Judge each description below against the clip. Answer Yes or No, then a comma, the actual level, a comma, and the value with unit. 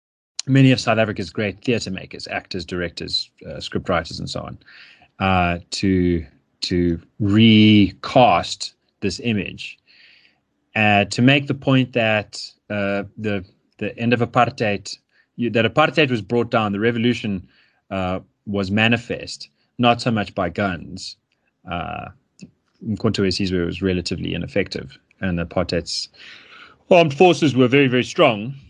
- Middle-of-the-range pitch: No, low, 105 Hz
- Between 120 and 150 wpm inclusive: Yes, slow, 135 wpm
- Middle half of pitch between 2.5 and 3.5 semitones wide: No, average, 4.4 semitones